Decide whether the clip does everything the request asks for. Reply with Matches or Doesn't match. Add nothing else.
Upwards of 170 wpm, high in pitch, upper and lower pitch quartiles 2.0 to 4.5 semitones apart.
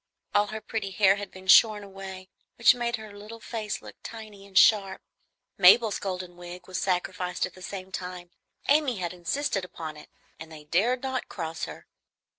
Matches